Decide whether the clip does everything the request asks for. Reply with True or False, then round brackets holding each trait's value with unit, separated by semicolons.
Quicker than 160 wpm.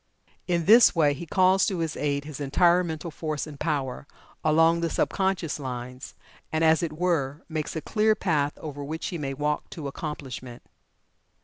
True (180 wpm)